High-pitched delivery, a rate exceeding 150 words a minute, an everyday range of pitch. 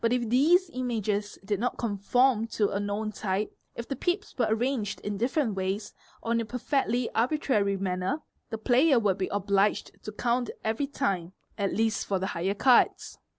Yes: high, 220 Hz; average, 180 wpm; average, 3.8 semitones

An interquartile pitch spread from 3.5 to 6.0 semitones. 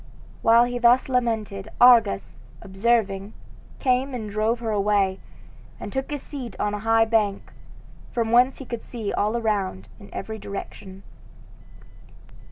No: average, 3.1 semitones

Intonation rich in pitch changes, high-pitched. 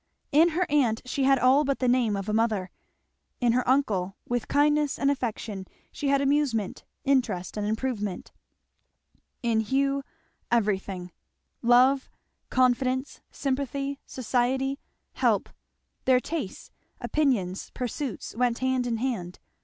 No: average, 3.9 semitones; very high, 255 Hz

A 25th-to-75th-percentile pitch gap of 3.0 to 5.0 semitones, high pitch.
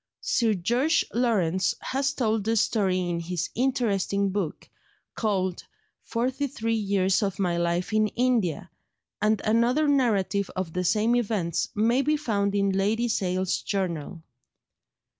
Yes: average, 4.0 semitones; high, 205 Hz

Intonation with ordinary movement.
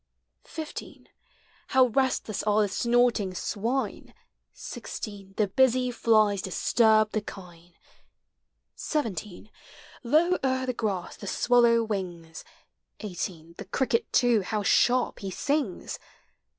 Yes: average, 4.2 semitones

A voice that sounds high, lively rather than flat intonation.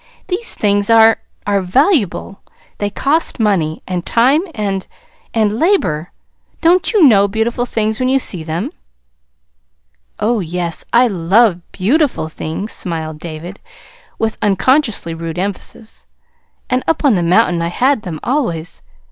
Yes: high, 205 Hz; wide, 6.1 semitones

